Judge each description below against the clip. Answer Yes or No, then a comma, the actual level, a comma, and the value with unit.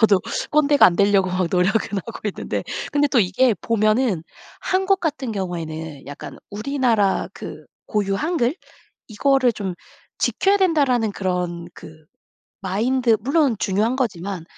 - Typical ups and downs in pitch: No, wide, 6.1 semitones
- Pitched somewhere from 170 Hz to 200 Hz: No, high, 215 Hz